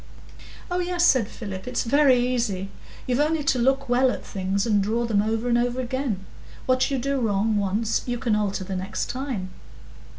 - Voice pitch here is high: Yes, high, 240 Hz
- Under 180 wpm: No, average, 190 wpm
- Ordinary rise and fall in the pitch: Yes, average, 4.2 semitones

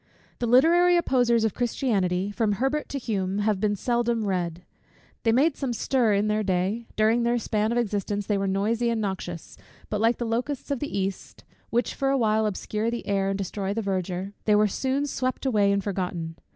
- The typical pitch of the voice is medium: No, high, 215 Hz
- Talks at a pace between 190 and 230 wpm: Yes, average, 200 wpm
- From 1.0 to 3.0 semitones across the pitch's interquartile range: No, average, 3.4 semitones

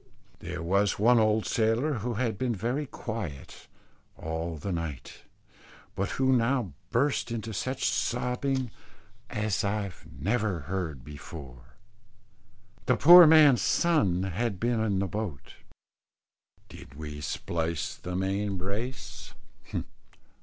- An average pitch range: No, wide, 6.0 semitones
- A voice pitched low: Yes, low, 105 Hz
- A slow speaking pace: Yes, slow, 115 wpm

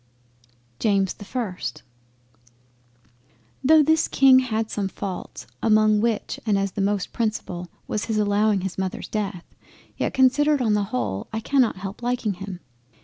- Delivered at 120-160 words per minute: Yes, average, 145 wpm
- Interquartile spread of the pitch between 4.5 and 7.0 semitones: No, average, 3.5 semitones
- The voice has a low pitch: No, high, 210 Hz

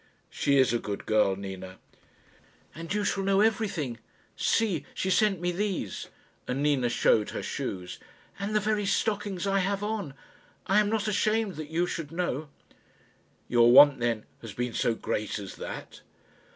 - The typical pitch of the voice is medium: Yes, medium, 165 Hz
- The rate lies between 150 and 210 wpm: Yes, average, 165 wpm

